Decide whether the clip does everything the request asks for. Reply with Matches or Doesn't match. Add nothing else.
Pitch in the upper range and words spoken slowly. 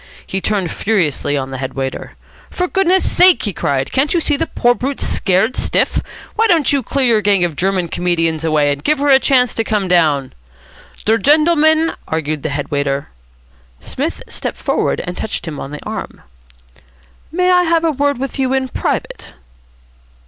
Doesn't match